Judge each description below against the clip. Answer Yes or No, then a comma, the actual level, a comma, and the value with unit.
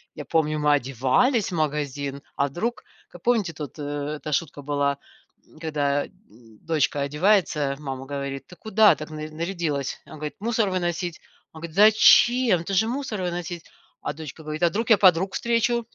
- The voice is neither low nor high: Yes, medium, 160 Hz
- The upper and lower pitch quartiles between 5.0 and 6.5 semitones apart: Yes, average, 5.3 semitones